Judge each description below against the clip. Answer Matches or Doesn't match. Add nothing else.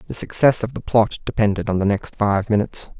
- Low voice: Matches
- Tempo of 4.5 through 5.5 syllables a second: Doesn't match